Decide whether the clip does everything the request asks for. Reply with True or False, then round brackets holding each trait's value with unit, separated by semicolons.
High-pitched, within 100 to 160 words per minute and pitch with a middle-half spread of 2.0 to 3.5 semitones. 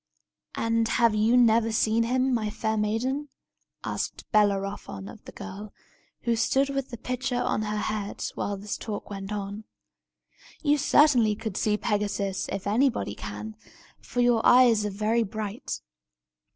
True (220 Hz; 150 wpm; 2.7 semitones)